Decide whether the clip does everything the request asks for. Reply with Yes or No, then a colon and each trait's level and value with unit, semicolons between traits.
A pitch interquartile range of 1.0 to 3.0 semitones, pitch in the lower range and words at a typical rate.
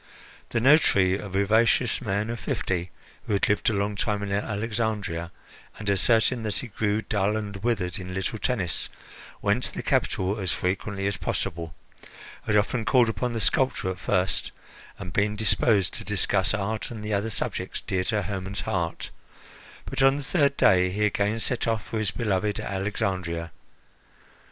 Yes: average, 2.7 semitones; low, 105 Hz; average, 170 wpm